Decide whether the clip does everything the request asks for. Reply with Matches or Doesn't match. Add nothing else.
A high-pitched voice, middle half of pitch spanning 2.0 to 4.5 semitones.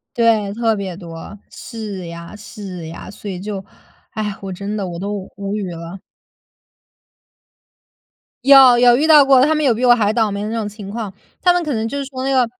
Matches